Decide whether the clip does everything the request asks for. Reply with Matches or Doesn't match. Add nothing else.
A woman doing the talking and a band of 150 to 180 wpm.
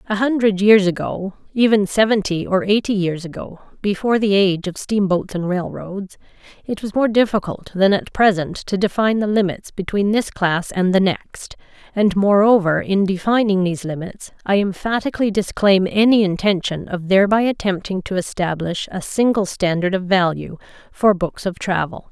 Matches